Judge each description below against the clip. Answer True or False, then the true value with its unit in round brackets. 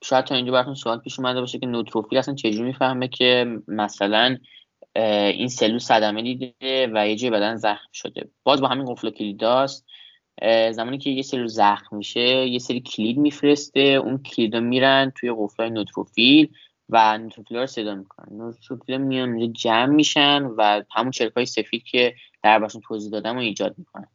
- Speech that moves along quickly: True (170 wpm)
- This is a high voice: False (120 Hz)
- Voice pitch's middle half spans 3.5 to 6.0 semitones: False (3.1 semitones)